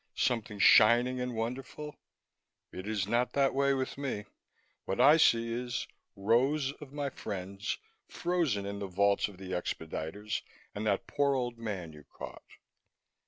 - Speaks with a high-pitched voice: No, low, 115 Hz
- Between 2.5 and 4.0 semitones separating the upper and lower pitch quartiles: No, average, 5.0 semitones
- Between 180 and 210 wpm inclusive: No, average, 150 wpm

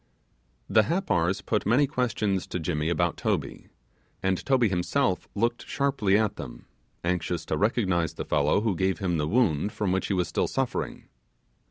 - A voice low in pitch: Yes, very low, 95 Hz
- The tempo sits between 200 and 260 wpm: No, average, 165 wpm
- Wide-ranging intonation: No, average, 4.7 semitones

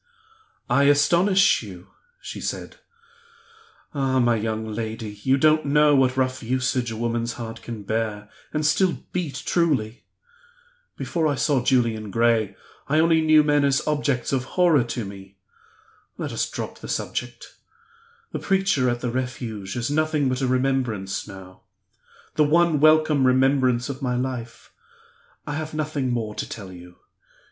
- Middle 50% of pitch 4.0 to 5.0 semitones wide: Yes, average, 4.6 semitones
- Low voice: Yes, low, 130 Hz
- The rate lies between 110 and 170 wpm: Yes, average, 150 wpm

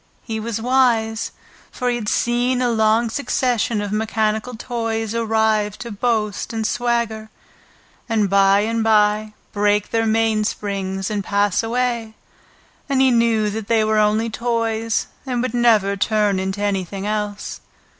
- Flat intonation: Yes, narrow, 2.0 semitones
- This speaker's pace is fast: No, average, 145 wpm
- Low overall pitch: No, high, 220 Hz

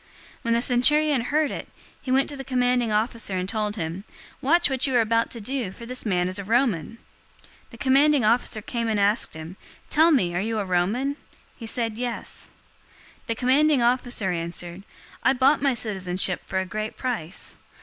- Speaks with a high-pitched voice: Yes, high, 230 Hz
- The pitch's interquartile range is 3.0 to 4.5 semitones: No, average, 5.0 semitones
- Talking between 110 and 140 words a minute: No, average, 195 wpm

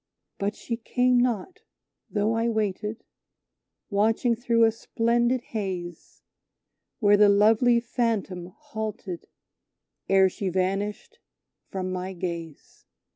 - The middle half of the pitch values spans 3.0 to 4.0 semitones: Yes, average, 3.4 semitones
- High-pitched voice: Yes, high, 210 Hz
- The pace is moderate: No, slow, 105 wpm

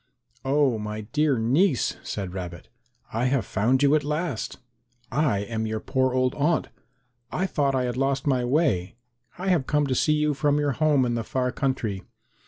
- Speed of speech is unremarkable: Yes, average, 185 wpm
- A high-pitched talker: No, low, 130 Hz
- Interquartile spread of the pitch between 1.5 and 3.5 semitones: No, average, 4.4 semitones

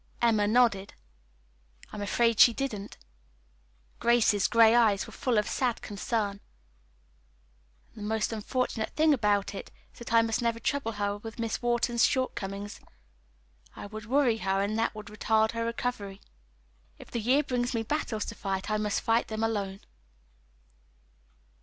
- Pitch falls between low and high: No, high, 225 Hz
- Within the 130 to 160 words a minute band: Yes, average, 155 wpm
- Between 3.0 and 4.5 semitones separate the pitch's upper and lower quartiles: No, narrow, 2.5 semitones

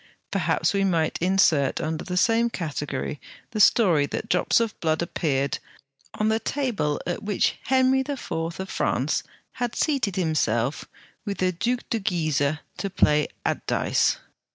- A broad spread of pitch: Yes, wide, 6.3 semitones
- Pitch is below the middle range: No, medium, 185 Hz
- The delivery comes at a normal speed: Yes, average, 150 wpm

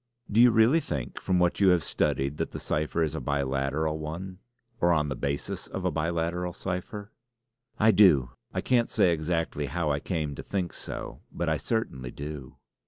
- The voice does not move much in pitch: No, average, 4.2 semitones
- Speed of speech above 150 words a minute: Yes, average, 185 wpm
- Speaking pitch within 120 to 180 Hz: No, very low, 80 Hz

